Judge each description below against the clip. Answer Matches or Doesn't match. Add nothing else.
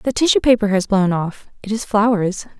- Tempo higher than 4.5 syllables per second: Matches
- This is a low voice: Doesn't match